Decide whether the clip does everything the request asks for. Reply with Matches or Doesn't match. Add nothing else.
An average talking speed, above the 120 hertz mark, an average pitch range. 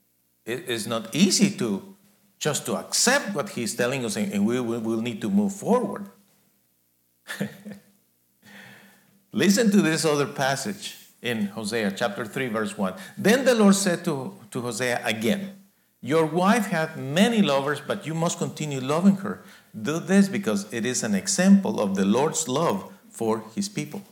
Doesn't match